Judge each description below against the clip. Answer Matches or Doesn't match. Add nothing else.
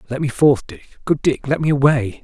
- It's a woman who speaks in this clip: Doesn't match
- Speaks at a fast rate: Matches